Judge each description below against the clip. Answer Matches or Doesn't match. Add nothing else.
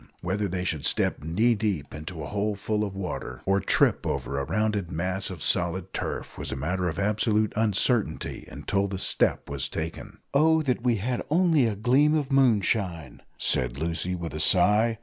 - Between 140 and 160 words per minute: Doesn't match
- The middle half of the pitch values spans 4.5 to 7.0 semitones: Matches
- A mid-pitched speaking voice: Doesn't match